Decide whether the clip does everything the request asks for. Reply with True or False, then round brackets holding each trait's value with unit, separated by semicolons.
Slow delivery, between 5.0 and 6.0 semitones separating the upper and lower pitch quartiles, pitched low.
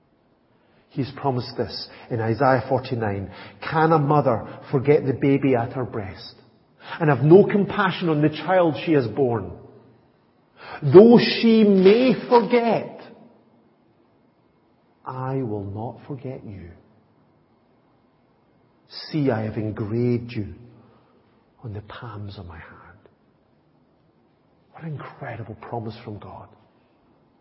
True (110 wpm; 5.4 semitones; 130 Hz)